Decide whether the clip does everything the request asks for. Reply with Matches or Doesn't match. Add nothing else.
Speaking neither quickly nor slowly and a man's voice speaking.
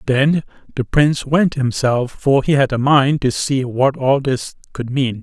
Matches